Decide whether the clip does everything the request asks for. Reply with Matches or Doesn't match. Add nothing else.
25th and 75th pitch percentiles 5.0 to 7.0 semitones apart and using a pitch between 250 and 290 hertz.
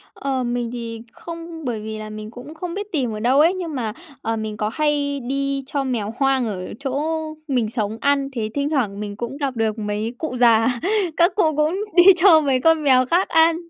Matches